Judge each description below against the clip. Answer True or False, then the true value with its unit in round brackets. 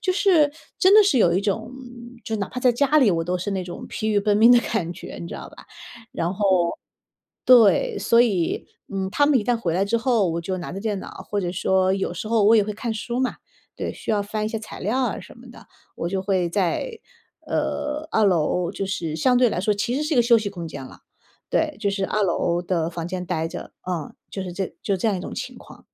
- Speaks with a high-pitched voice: True (205 Hz)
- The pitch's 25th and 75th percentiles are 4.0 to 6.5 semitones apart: True (4.9 semitones)